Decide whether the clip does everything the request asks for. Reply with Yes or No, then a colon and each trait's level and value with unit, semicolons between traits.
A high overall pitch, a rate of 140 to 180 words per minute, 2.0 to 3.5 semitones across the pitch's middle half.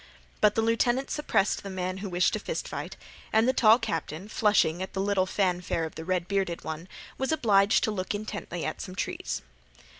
No: high, 195 Hz; average, 200 wpm; average, 3.2 semitones